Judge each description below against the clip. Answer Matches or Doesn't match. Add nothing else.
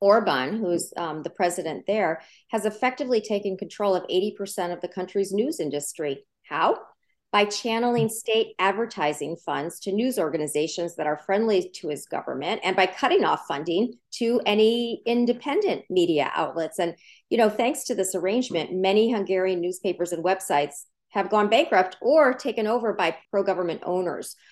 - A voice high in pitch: Matches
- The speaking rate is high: Doesn't match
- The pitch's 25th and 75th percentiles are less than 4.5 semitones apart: Matches